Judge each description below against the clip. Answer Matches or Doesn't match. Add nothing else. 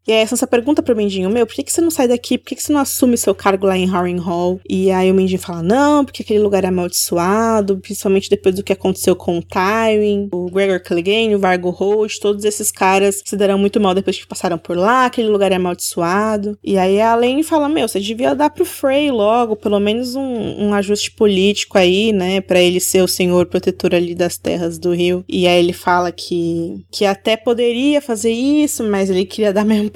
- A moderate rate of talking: Doesn't match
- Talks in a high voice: Matches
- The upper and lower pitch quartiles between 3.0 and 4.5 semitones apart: Matches